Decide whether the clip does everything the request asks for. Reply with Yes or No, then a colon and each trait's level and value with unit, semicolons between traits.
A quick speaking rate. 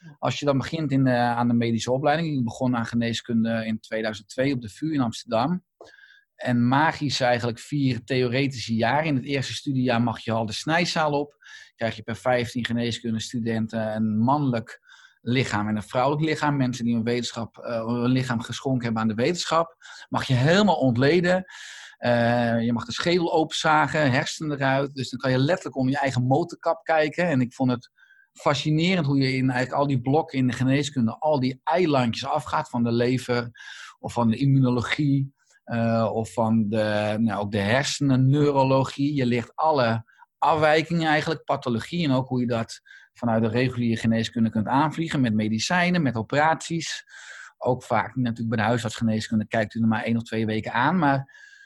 No: average, 180 wpm